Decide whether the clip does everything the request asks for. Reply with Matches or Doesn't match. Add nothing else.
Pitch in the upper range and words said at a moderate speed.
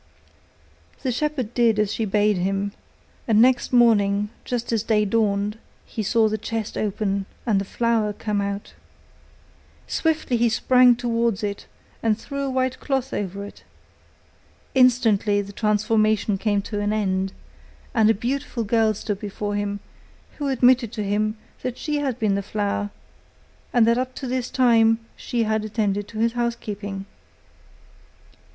Matches